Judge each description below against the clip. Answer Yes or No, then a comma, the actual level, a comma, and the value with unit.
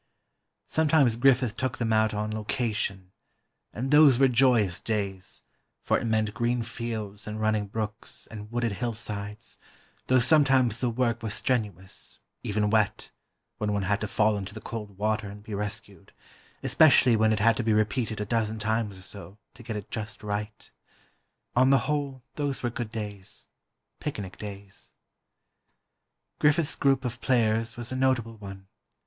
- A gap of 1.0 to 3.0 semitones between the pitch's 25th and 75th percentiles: Yes, average, 2.7 semitones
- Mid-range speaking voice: No, low, 110 Hz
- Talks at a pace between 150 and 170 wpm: Yes, average, 155 wpm